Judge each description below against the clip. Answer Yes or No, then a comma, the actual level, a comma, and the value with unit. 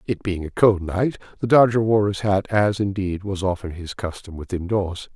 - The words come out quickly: Yes, fast, 210 wpm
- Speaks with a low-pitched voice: Yes, low, 100 Hz